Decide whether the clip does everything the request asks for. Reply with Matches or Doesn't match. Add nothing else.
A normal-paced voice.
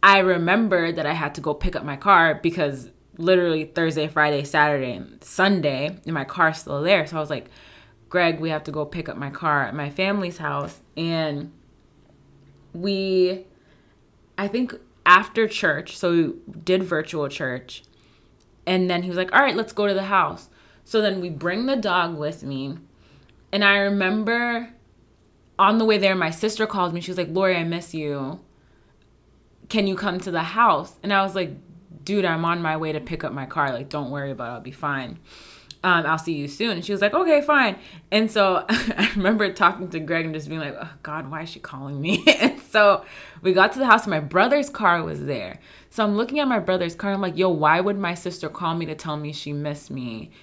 Doesn't match